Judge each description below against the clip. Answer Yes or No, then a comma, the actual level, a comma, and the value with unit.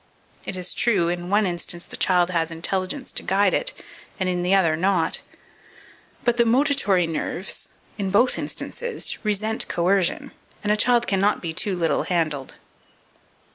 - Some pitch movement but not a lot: Yes, average, 3.6 semitones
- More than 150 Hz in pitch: Yes, high, 190 Hz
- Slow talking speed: No, average, 155 wpm